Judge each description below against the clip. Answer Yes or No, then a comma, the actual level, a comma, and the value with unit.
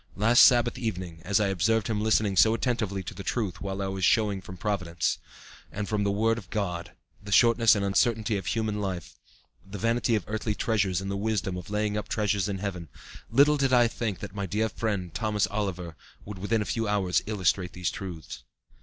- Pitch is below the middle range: Yes, low, 105 Hz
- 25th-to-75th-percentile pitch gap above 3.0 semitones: No, narrow, 2.6 semitones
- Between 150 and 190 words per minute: No, fast, 205 wpm